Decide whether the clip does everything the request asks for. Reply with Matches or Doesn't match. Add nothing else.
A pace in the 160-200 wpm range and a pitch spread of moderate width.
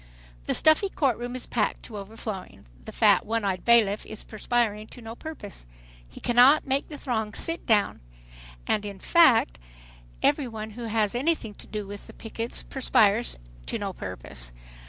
Matches